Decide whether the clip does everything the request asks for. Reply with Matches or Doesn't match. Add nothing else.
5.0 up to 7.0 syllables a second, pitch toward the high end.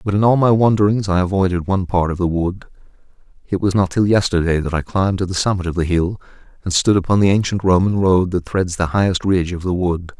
Doesn't match